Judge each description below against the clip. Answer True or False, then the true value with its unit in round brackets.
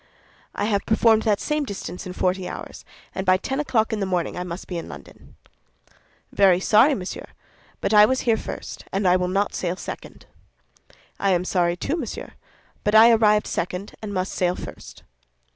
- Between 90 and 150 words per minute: False (180 wpm)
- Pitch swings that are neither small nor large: True (3.3 semitones)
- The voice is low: False (200 Hz)